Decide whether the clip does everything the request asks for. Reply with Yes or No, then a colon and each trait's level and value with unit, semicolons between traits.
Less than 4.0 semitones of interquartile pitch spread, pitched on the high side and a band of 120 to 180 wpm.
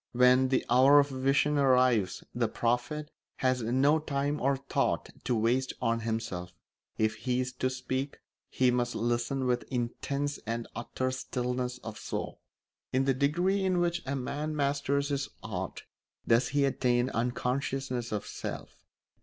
No: narrow, 2.5 semitones; low, 130 Hz; average, 150 wpm